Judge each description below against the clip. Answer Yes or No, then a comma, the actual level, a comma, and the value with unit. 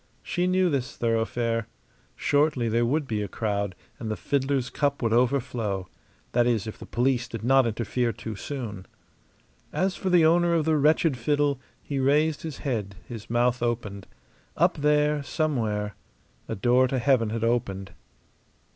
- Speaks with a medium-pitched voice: No, low, 125 Hz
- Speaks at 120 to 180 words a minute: Yes, average, 160 wpm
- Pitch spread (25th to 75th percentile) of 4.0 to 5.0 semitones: Yes, average, 4.4 semitones